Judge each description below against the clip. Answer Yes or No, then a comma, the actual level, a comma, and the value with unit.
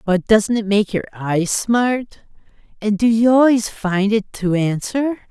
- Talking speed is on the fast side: No, average, 170 wpm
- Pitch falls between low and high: No, high, 215 Hz